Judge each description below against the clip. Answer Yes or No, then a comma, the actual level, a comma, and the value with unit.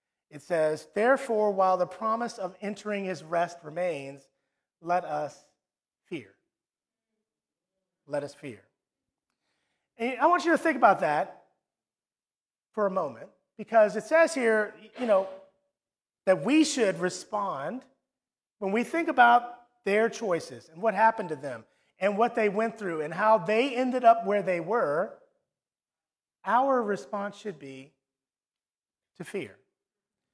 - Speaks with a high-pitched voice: Yes, high, 210 Hz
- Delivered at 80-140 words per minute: Yes, slow, 135 wpm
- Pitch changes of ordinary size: Yes, average, 4.7 semitones